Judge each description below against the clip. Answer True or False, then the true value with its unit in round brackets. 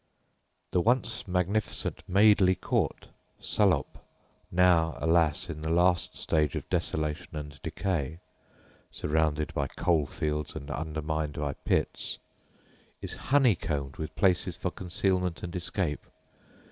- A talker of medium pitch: False (80 Hz)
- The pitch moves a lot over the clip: False (3.3 semitones)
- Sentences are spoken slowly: True (115 wpm)